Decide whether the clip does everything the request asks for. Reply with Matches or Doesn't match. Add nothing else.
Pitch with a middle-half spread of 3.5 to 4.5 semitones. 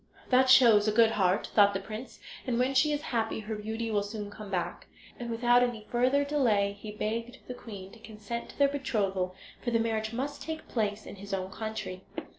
Doesn't match